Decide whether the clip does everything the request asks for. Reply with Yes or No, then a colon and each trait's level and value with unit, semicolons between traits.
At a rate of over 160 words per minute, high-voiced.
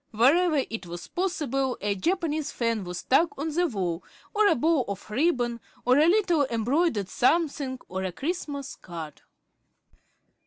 No: average, 150 wpm; very high, 270 Hz